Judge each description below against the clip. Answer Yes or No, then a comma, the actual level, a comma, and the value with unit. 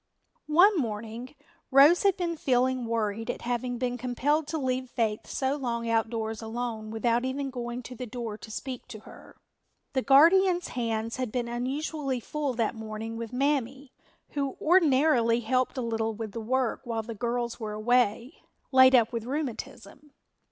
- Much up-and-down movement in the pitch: No, average, 3.0 semitones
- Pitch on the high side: Yes, high, 245 Hz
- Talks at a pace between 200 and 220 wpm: No, average, 165 wpm